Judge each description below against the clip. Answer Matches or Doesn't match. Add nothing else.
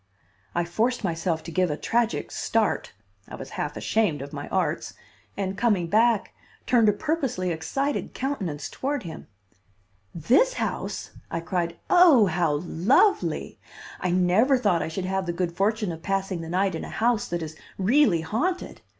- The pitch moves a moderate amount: Doesn't match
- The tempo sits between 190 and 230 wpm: Doesn't match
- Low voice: Doesn't match